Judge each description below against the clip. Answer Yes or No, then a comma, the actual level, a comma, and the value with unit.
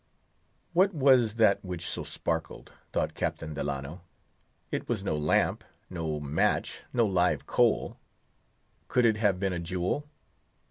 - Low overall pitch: Yes, very low, 90 Hz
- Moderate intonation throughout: No, wide, 6.0 semitones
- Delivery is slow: Yes, slow, 125 wpm